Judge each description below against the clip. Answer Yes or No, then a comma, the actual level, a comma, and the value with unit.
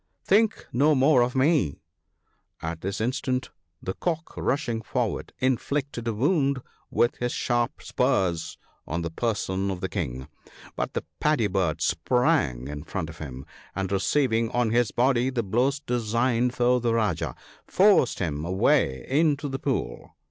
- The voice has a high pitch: No, low, 120 Hz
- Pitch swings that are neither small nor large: No, wide, 6.2 semitones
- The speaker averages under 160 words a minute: Yes, average, 150 wpm